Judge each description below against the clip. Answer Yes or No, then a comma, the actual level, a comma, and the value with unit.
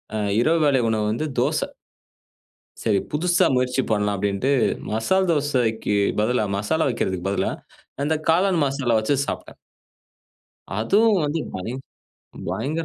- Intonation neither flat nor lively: No, wide, 6.8 semitones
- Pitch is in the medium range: No, low, 130 Hz